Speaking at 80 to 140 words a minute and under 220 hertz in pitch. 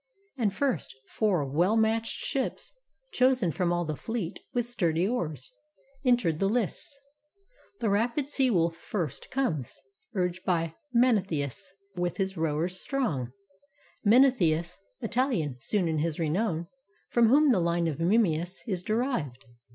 Yes: slow, 135 wpm; medium, 185 Hz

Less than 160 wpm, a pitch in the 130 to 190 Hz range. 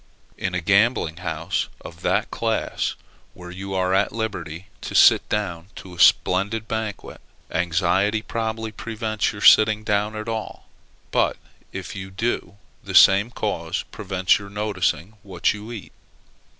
No: average, 145 wpm; low, 100 Hz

